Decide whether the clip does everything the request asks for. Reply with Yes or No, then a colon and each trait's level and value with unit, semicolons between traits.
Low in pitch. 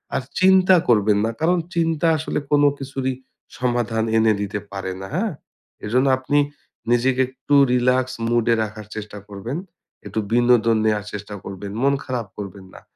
Yes: low, 120 Hz